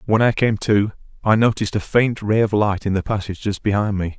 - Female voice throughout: No, male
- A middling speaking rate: No, fast, 245 wpm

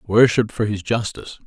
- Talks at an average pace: Yes, average, 165 wpm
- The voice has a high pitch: No, low, 110 Hz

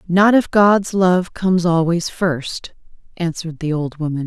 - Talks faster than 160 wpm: No, average, 155 wpm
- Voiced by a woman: Yes, female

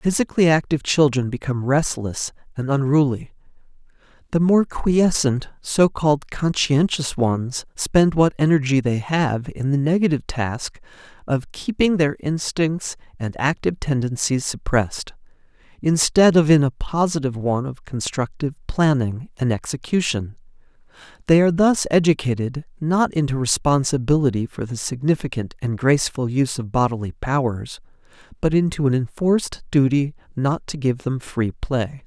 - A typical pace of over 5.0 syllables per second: No, 4.9 syllables/s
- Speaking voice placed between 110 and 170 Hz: Yes, medium, 140 Hz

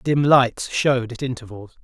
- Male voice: Yes, male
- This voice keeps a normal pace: Yes, average, 165 wpm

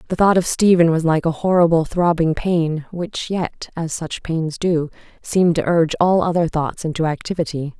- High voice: No, medium, 165 Hz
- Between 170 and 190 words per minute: Yes, average, 185 wpm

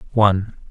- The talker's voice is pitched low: Yes, low, 100 Hz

